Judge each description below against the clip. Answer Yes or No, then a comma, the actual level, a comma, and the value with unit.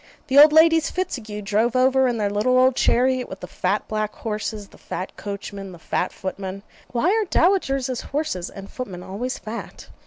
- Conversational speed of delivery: Yes, average, 180 wpm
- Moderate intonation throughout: Yes, average, 4.8 semitones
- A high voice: Yes, high, 230 Hz